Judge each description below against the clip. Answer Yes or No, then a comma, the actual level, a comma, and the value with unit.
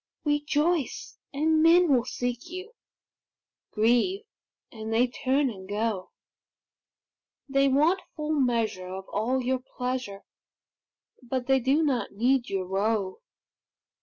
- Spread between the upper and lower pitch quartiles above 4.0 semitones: Yes, average, 4.9 semitones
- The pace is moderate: No, slow, 115 wpm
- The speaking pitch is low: No, very high, 255 Hz